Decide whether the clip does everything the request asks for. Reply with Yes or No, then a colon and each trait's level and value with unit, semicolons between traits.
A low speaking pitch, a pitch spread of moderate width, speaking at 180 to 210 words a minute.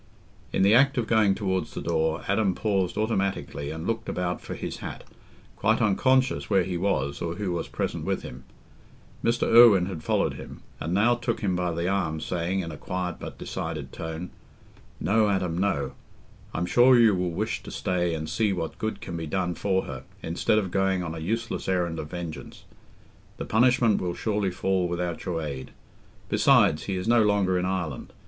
Yes: very low, 95 Hz; average, 3.6 semitones; average, 190 wpm